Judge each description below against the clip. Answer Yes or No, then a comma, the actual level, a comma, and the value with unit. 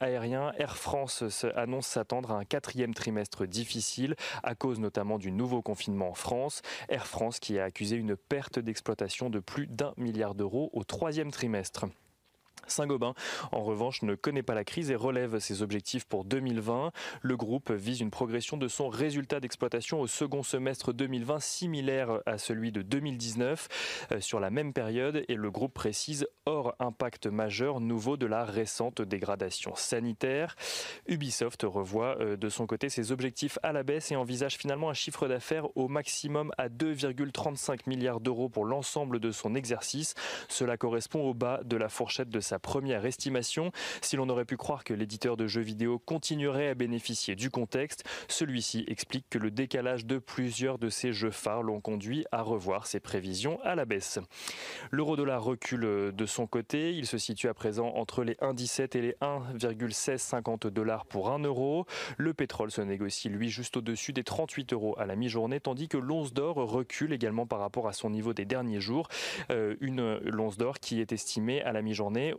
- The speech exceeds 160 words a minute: Yes, average, 180 wpm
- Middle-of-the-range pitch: No, low, 125 Hz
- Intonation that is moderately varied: Yes, average, 3.6 semitones